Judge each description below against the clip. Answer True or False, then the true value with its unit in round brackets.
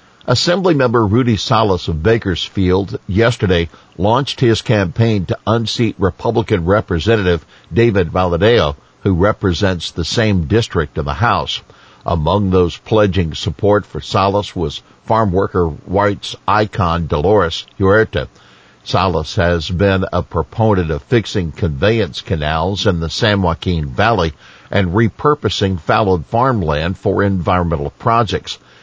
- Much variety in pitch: False (4.3 semitones)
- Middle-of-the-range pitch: False (100 Hz)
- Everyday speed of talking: False (120 wpm)